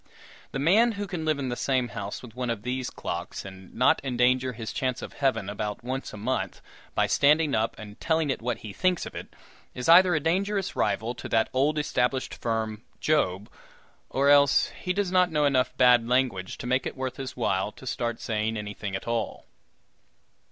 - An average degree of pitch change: Yes, average, 4.6 semitones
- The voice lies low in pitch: Yes, low, 125 Hz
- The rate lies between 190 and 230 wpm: Yes, average, 200 wpm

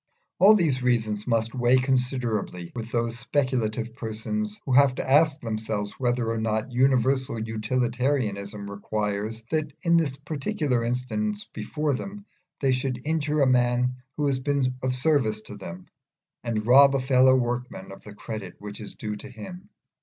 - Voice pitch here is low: Yes, low, 125 Hz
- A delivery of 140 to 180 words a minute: Yes, average, 160 wpm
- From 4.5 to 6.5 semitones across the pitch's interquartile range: No, average, 3.9 semitones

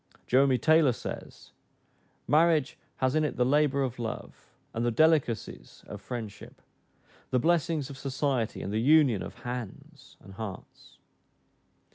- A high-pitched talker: No, low, 130 Hz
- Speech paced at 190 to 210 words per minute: No, slow, 135 wpm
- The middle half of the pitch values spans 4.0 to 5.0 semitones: Yes, average, 4.4 semitones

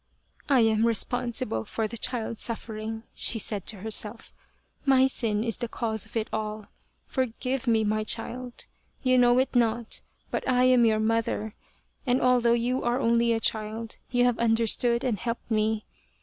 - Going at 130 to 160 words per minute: No, average, 175 wpm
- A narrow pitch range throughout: Yes, narrow, 2.0 semitones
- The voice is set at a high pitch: Yes, high, 230 Hz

